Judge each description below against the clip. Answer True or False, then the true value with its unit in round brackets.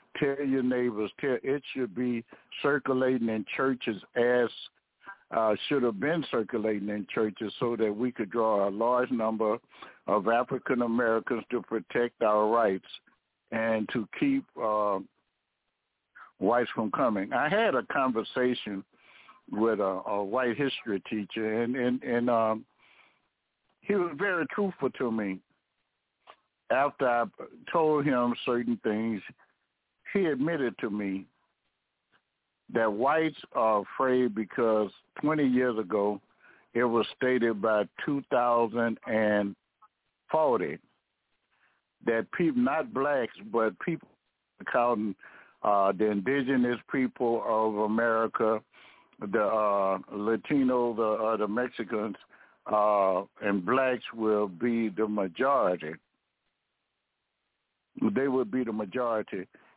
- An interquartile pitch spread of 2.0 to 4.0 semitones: True (2.9 semitones)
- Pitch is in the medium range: False (115 Hz)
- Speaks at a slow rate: True (115 wpm)